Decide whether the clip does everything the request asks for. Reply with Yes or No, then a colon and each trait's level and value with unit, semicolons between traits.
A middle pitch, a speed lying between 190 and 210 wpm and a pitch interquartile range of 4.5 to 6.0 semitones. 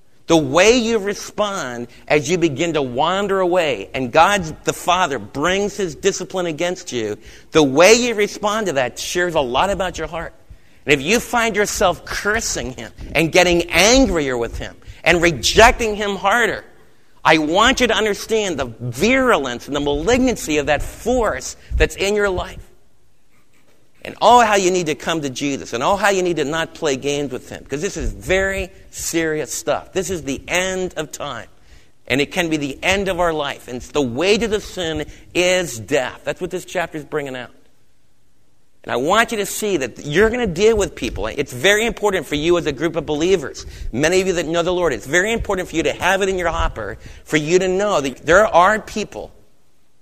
Yes: medium, 175 Hz; fast, 205 wpm; average, 5.2 semitones